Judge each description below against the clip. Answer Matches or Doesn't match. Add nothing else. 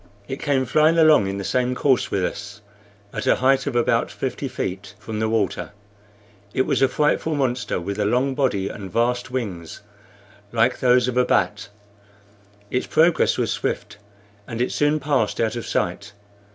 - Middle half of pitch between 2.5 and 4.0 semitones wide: Doesn't match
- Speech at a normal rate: Matches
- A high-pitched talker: Doesn't match